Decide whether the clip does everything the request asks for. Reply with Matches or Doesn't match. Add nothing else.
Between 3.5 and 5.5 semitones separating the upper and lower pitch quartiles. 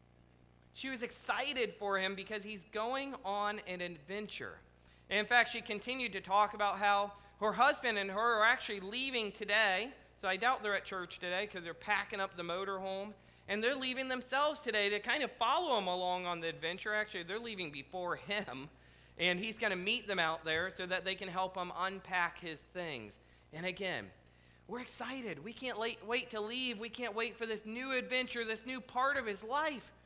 Matches